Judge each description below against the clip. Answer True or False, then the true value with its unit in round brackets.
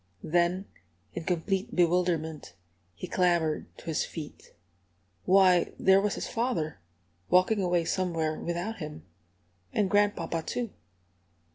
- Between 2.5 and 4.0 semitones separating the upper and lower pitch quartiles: True (3.0 semitones)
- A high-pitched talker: False (175 Hz)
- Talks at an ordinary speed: False (115 wpm)